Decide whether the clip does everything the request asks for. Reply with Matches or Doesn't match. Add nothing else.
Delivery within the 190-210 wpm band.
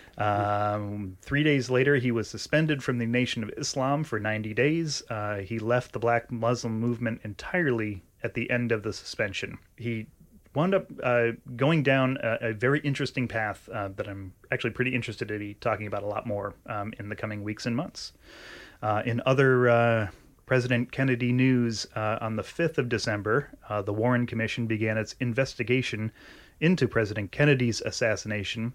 Doesn't match